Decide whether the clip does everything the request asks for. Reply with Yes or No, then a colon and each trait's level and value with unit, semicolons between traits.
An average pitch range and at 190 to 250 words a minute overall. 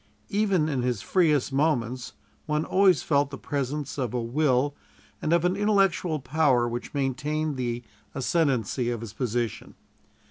No: average, 4.2 semitones; average, 145 wpm